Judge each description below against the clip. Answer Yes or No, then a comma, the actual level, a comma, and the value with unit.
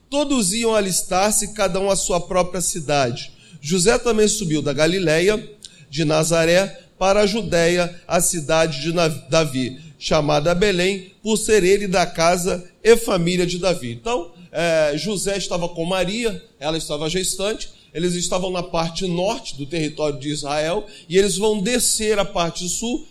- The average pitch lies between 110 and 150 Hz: No, medium, 180 Hz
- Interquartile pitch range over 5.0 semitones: No, average, 3.9 semitones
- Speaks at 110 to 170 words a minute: Yes, average, 150 wpm